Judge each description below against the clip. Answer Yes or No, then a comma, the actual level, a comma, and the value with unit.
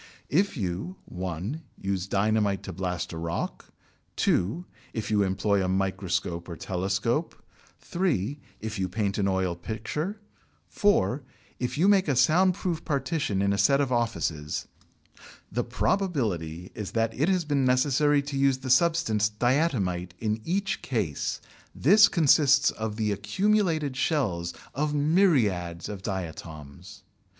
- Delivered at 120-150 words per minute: Yes, average, 140 wpm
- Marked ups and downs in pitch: Yes, wide, 7.9 semitones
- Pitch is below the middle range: Yes, low, 110 Hz